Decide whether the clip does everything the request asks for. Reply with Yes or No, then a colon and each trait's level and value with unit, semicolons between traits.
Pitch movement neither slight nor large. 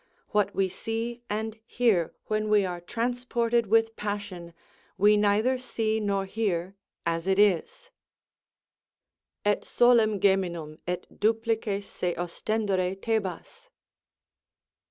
Yes: average, 3.0 semitones